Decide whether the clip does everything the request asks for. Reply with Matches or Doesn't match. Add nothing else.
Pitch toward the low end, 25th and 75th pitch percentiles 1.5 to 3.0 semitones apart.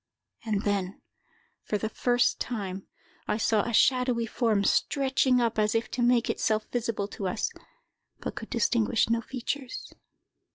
Doesn't match